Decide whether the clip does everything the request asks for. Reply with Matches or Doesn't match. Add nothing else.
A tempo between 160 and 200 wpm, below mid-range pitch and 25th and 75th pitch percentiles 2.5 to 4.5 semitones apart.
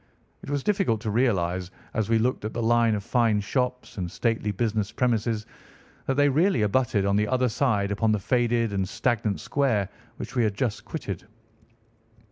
Matches